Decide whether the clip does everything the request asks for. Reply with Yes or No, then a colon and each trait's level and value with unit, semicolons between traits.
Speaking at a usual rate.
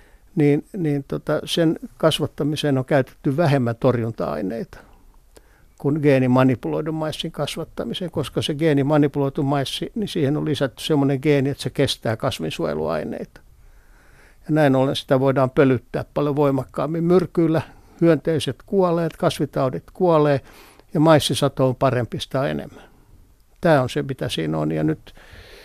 Yes: average, 125 wpm